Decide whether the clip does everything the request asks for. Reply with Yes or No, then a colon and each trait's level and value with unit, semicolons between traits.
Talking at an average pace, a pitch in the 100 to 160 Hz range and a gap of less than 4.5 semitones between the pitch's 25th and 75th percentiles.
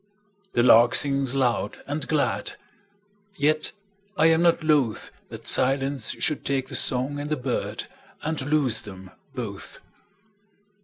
No: slow, 115 wpm; medium, 140 Hz; average, 3.3 semitones